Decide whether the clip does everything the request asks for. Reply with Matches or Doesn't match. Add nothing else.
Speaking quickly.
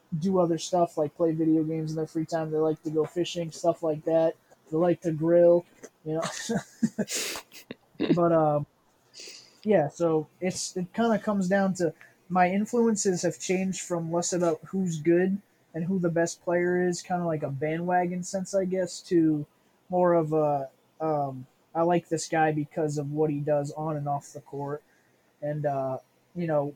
Doesn't match